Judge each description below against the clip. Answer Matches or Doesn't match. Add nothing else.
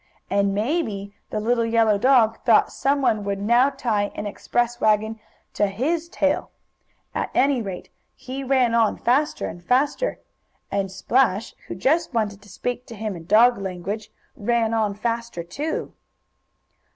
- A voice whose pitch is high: Matches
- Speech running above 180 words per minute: Doesn't match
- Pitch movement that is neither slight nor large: Matches